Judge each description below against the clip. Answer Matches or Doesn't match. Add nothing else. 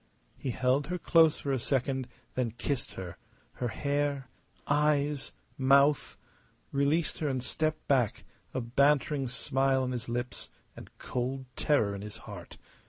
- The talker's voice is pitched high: Doesn't match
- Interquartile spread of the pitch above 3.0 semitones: Doesn't match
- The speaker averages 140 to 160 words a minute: Matches